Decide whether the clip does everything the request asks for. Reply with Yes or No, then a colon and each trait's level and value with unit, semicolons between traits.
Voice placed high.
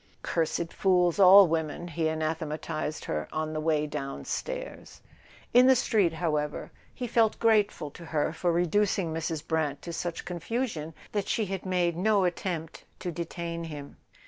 No: medium, 170 Hz